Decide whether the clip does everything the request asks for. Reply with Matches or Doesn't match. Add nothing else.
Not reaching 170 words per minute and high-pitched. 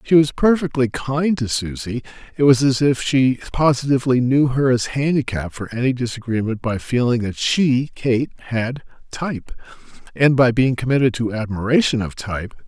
Doesn't match